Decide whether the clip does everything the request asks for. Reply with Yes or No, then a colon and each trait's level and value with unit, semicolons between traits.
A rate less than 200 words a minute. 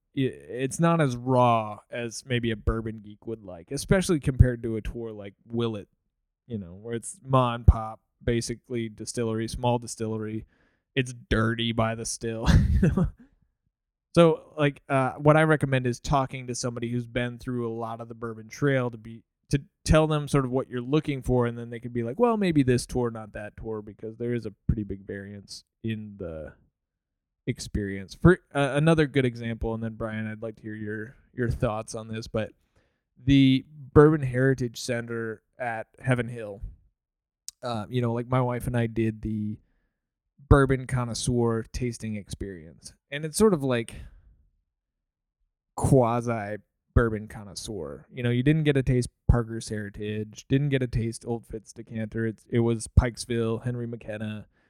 Yes: average, 170 wpm